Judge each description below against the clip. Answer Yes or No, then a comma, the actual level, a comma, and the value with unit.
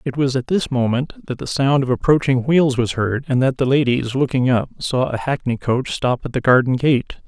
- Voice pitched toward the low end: Yes, low, 130 Hz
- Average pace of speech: No, fast, 230 wpm